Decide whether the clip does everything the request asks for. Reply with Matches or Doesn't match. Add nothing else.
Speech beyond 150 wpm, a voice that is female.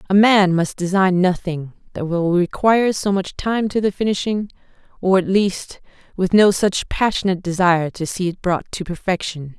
Matches